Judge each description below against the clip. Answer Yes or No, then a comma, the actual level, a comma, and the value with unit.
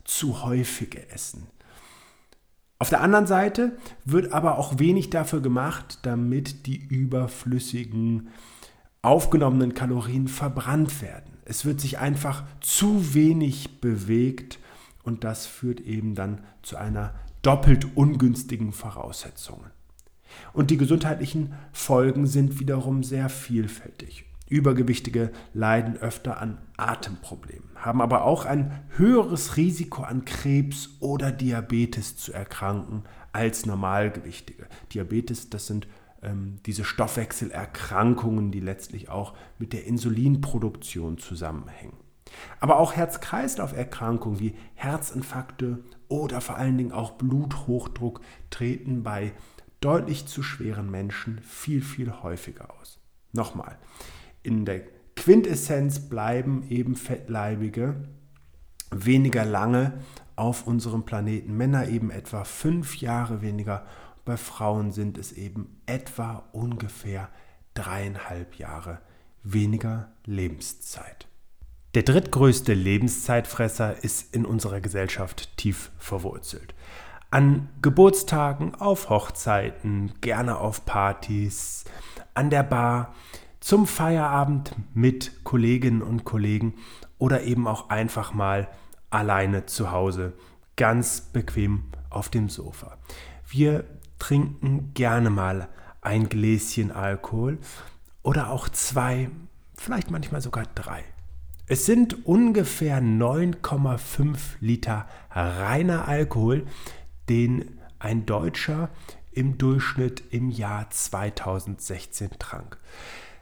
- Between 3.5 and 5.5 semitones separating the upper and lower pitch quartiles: Yes, average, 4.6 semitones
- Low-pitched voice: Yes, low, 120 Hz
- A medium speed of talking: No, slow, 105 wpm